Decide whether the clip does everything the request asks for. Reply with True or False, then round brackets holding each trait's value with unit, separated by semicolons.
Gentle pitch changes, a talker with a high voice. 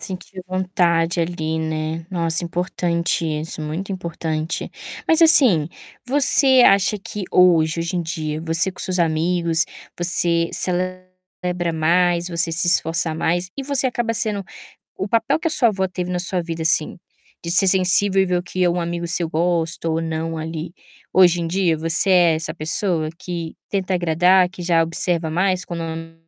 False (2.0 semitones; 175 Hz)